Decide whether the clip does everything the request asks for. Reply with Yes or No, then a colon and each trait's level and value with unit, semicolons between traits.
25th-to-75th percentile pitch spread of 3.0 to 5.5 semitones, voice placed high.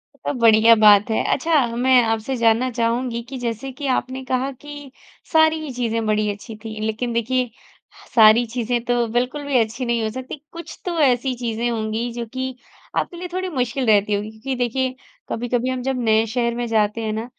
No: narrow, 2.6 semitones; high, 240 Hz